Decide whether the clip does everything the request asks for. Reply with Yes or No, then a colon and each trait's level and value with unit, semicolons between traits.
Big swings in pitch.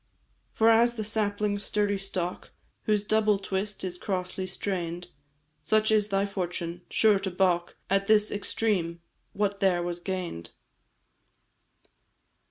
No: average, 2.8 semitones